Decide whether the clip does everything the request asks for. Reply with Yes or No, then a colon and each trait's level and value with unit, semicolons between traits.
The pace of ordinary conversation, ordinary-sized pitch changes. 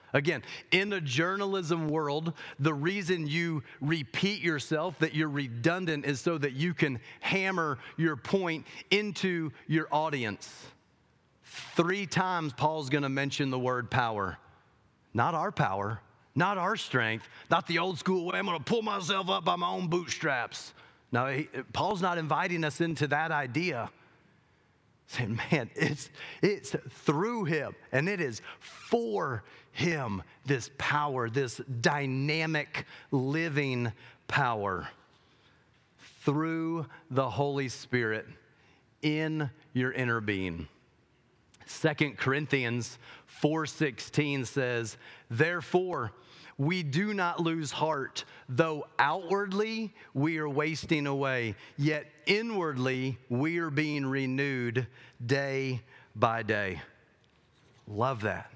No: slow, 120 wpm; average, 4.5 semitones